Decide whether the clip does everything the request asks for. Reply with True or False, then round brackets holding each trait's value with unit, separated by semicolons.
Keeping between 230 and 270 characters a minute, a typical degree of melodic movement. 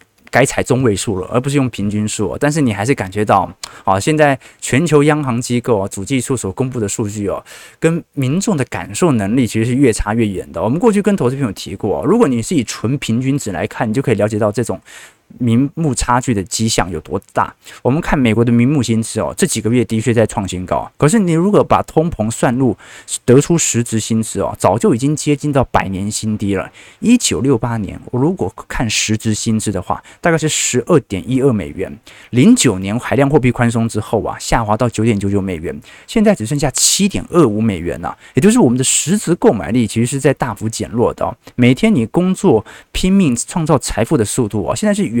False (325 characters per minute; 5.0 semitones)